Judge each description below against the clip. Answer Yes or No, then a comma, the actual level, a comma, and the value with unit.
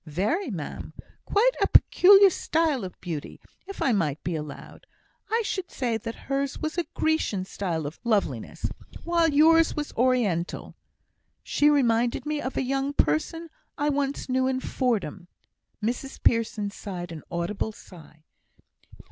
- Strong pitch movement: Yes, wide, 8.6 semitones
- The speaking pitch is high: Yes, high, 245 Hz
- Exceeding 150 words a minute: No, average, 145 wpm